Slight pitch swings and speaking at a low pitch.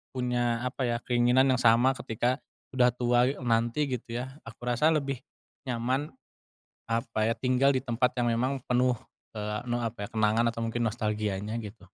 Yes: narrow, 1.9 semitones; low, 120 Hz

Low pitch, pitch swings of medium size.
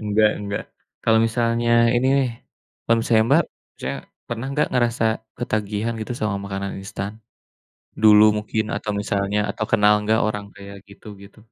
No: low, 110 Hz; narrow, 2.2 semitones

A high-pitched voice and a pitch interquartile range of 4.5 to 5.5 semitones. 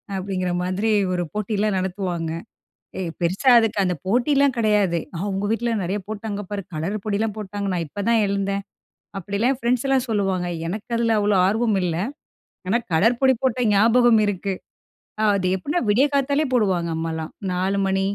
No: high, 205 Hz; average, 3.5 semitones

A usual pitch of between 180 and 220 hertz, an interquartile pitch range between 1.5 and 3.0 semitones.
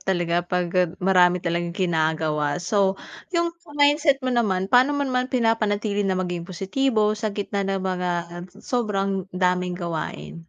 No: high, 190 Hz; average, 4.2 semitones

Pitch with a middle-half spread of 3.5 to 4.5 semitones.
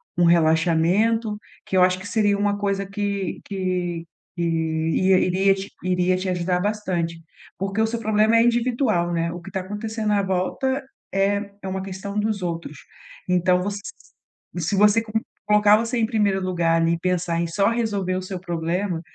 No: average, 2.9 semitones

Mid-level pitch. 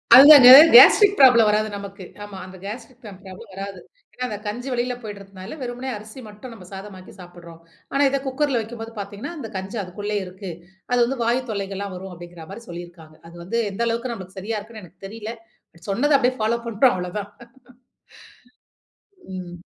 No: high, 210 Hz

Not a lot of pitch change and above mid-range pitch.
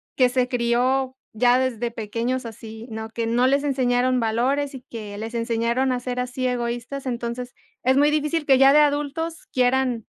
Yes: narrow, 2.2 semitones; very high, 250 Hz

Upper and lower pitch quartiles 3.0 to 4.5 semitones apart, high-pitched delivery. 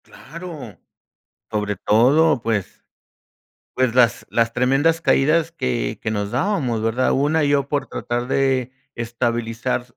No: average, 4.0 semitones; low, 125 Hz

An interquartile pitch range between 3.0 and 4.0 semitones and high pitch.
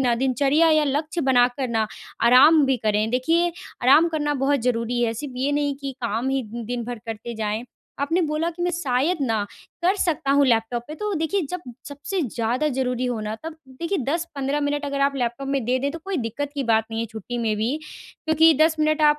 No: average, 4.4 semitones; very high, 275 Hz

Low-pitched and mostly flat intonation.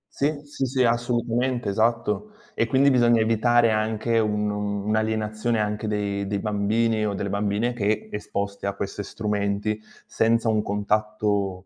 Yes: low, 110 Hz; narrow, 2.2 semitones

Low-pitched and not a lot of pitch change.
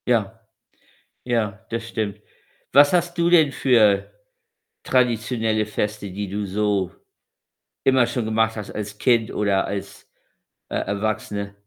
No: low, 110 Hz; average, 3.0 semitones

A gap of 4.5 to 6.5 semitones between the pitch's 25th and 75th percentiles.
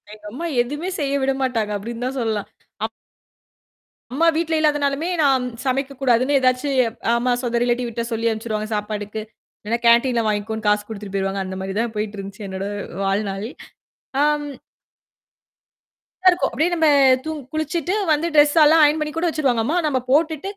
Yes: wide, 5.5 semitones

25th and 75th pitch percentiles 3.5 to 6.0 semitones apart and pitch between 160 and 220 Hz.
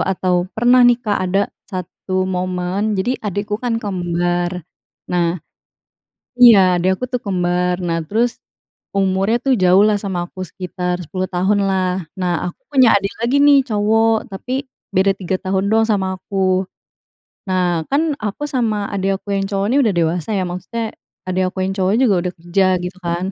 No: average, 3.1 semitones; high, 190 Hz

